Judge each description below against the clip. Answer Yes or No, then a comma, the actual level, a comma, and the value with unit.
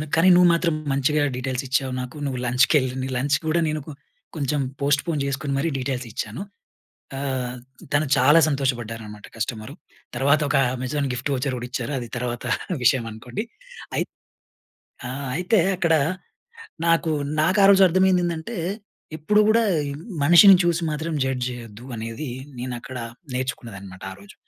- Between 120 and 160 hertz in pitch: Yes, low, 135 Hz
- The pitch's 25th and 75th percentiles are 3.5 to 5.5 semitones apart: Yes, average, 4.2 semitones